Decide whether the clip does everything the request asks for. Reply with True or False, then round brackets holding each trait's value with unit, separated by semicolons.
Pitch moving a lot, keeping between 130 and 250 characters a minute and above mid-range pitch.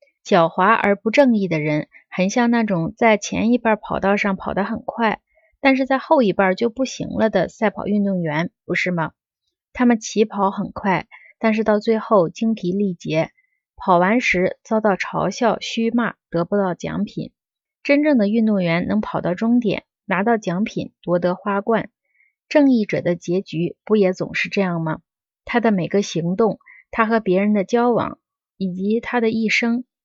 False (4.0 semitones; 245 characters per minute; 210 Hz)